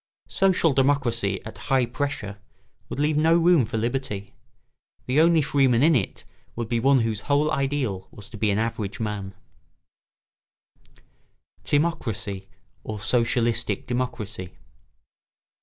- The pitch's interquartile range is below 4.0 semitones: No, average, 4.9 semitones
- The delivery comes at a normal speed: No, slow, 125 wpm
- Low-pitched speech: Yes, low, 120 Hz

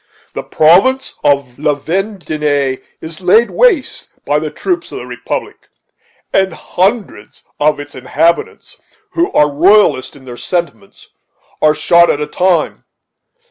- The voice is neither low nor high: Yes, medium, 165 Hz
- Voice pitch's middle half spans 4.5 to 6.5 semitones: Yes, average, 5.3 semitones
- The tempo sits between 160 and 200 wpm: No, slow, 135 wpm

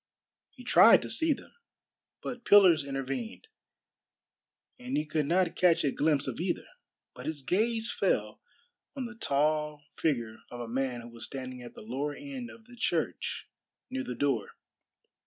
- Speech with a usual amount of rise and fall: No, wide, 9.0 semitones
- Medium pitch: Yes, medium, 150 Hz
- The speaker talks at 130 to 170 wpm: Yes, average, 160 wpm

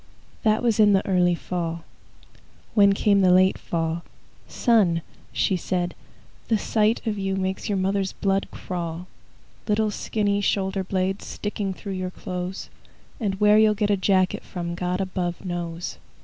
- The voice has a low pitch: No, high, 190 Hz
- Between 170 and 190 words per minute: No, average, 150 wpm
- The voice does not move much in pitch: Yes, narrow, 2.3 semitones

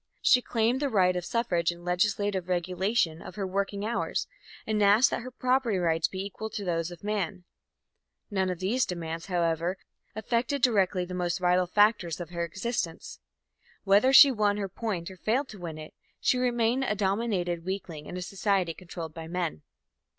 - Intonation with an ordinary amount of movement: Yes, average, 3.8 semitones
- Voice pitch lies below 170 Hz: No, high, 190 Hz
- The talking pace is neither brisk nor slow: Yes, average, 180 wpm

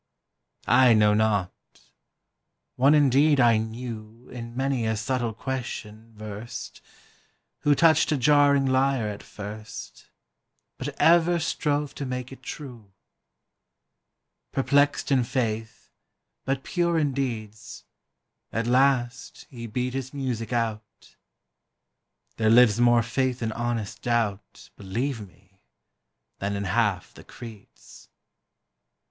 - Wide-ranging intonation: No, average, 3.7 semitones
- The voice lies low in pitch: Yes, low, 120 Hz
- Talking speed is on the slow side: Yes, slow, 115 wpm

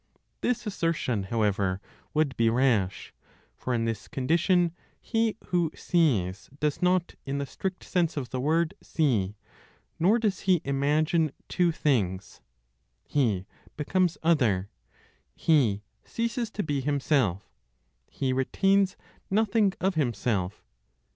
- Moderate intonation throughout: No, wide, 7.6 semitones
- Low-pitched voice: No, medium, 145 Hz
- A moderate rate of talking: No, slow, 120 wpm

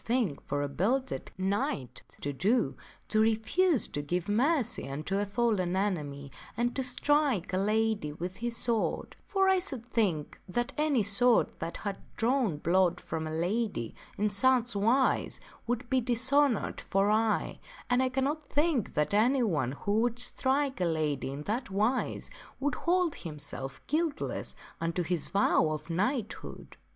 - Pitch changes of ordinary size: No, wide, 6.6 semitones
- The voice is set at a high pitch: Yes, high, 215 Hz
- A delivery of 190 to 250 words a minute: No, average, 155 wpm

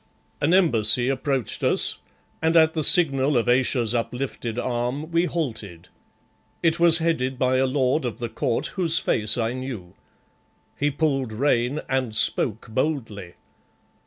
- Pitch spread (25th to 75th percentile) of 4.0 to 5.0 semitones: Yes, average, 4.5 semitones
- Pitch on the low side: Yes, low, 130 Hz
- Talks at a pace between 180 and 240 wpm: No, average, 140 wpm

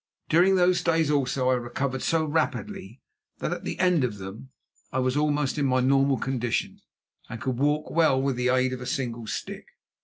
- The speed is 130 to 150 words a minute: No, average, 190 wpm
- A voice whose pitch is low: Yes, low, 130 Hz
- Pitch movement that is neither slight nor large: Yes, average, 3.2 semitones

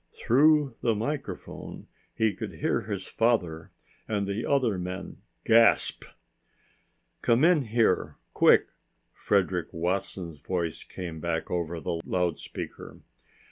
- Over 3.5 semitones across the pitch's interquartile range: Yes, average, 5.2 semitones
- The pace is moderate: No, slow, 110 wpm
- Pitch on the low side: Yes, low, 100 Hz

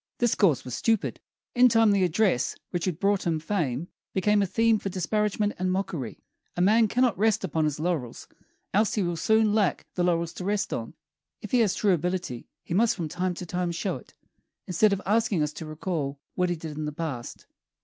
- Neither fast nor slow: No, fast, 210 wpm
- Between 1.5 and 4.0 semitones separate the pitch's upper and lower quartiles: No, average, 4.5 semitones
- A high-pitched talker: No, medium, 180 Hz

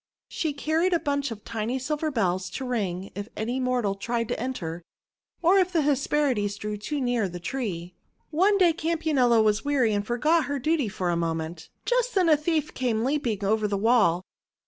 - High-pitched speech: Yes, high, 245 Hz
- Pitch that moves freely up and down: Yes, wide, 6.7 semitones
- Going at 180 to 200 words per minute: Yes, average, 190 wpm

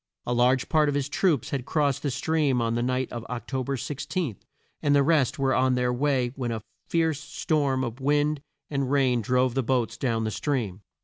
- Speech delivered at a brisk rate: Yes, fast, 210 wpm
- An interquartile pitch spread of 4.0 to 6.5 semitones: No, average, 2.9 semitones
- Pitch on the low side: Yes, low, 130 Hz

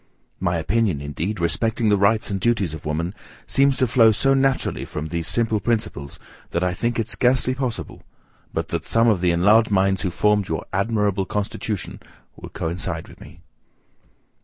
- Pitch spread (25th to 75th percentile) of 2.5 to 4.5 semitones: No, average, 4.9 semitones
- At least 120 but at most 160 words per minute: No, average, 170 wpm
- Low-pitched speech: Yes, low, 100 Hz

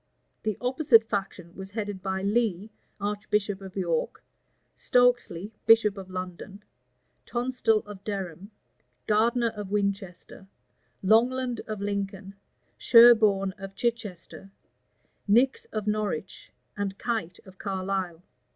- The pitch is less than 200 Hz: No, high, 205 Hz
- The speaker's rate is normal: No, slow, 105 wpm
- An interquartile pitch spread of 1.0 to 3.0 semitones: Yes, average, 2.7 semitones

